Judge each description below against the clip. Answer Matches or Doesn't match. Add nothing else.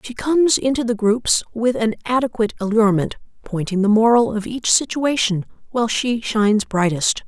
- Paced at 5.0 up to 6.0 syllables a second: Matches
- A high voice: Matches